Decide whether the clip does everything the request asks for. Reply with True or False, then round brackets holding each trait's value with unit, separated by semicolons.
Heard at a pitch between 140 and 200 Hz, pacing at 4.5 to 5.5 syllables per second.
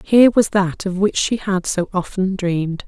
True (190 Hz; 4.8 syllables/s)